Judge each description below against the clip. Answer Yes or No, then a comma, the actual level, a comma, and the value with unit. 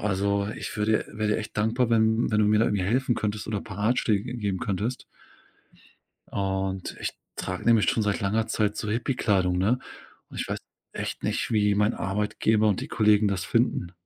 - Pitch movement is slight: Yes, narrow, 1.9 semitones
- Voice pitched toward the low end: Yes, low, 105 Hz